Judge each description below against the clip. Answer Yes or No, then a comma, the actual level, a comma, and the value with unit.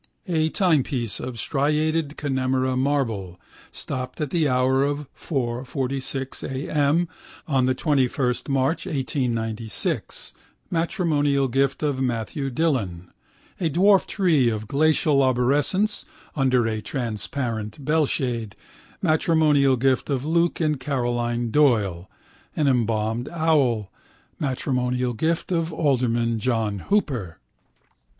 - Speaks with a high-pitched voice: No, low, 135 Hz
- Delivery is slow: Yes, slow, 105 wpm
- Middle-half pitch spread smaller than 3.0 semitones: No, average, 4.1 semitones